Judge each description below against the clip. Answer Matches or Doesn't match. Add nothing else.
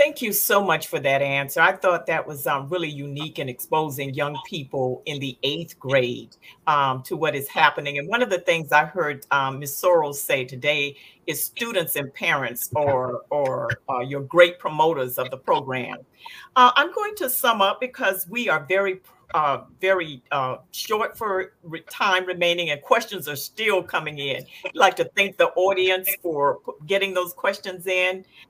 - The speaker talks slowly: Doesn't match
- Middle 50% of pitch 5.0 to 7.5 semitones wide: Matches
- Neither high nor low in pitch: Matches